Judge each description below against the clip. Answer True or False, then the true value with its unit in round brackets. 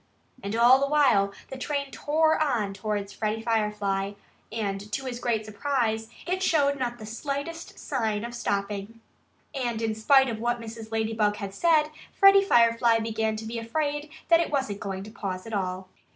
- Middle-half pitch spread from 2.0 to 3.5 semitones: False (4.7 semitones)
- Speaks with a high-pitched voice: True (230 Hz)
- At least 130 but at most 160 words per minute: False (170 wpm)